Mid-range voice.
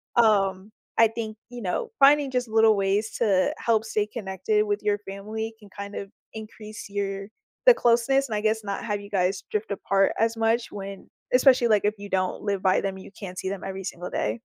No: high, 210 Hz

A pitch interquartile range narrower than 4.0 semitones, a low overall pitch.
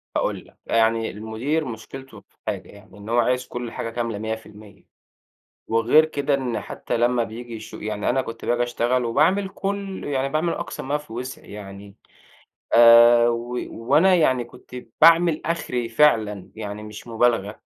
Yes: average, 3.6 semitones; low, 120 Hz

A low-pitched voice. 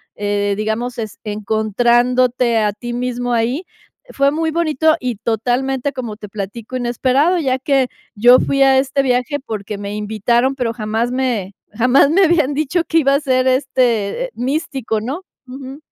No: very high, 250 Hz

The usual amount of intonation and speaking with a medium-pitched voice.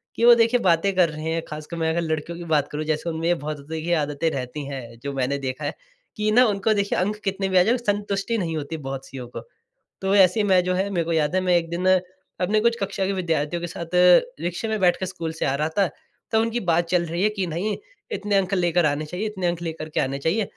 Yes: average, 4.1 semitones; medium, 175 Hz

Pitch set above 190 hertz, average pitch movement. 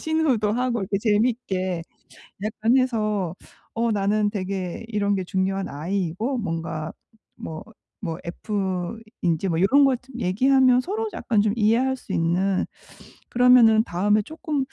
Yes: high, 210 Hz; average, 4.7 semitones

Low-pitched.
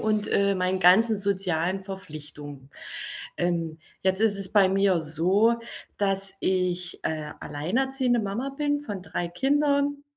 No: high, 195 Hz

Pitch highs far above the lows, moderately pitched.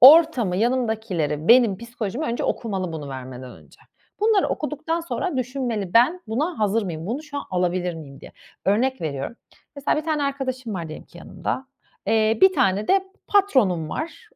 No: wide, 7.9 semitones; high, 230 Hz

